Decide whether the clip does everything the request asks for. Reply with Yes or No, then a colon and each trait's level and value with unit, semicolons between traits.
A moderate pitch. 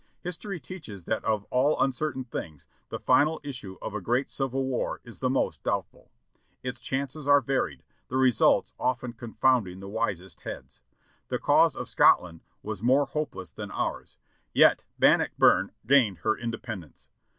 No: low, 125 Hz